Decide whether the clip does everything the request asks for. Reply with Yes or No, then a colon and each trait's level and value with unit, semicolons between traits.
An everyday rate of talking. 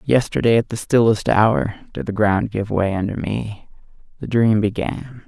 Yes: average, 170 wpm